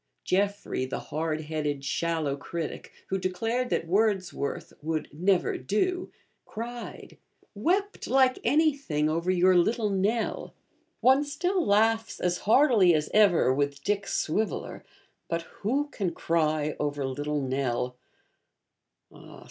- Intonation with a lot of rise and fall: Yes, wide, 6.7 semitones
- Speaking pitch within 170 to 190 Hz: Yes, medium, 185 Hz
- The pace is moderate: No, slow, 115 wpm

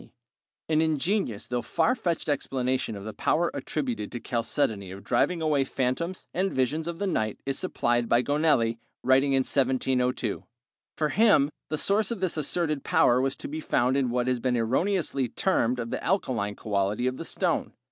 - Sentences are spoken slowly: No, average, 180 wpm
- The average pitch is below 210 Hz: Yes, low, 135 Hz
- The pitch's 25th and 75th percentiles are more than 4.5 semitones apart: Yes, average, 4.9 semitones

